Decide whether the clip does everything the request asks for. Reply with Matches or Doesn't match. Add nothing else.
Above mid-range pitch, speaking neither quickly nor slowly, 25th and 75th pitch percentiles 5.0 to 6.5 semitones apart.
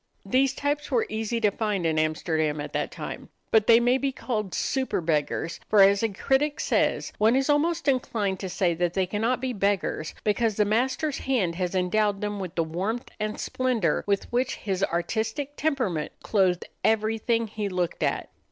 Matches